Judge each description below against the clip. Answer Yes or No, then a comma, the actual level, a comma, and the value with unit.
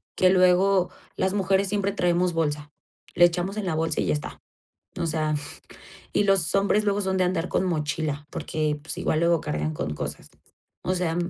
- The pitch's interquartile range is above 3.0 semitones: Yes, average, 3.4 semitones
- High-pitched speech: No, medium, 175 Hz